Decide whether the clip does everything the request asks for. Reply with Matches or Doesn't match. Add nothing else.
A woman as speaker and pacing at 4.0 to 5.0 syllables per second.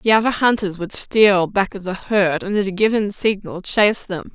Matches